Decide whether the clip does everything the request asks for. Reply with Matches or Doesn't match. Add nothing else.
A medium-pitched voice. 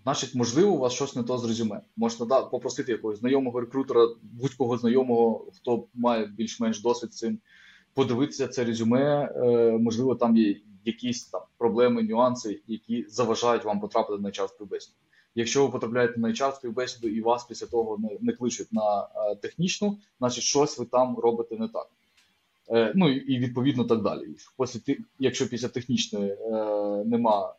Doesn't match